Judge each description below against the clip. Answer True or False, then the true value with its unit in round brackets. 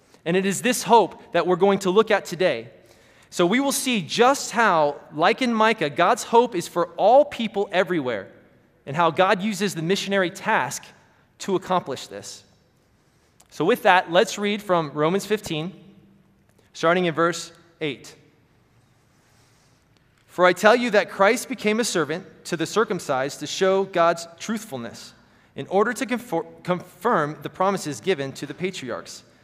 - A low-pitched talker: False (175 Hz)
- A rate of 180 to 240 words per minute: False (155 wpm)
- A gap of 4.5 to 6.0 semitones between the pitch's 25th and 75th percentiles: True (5.5 semitones)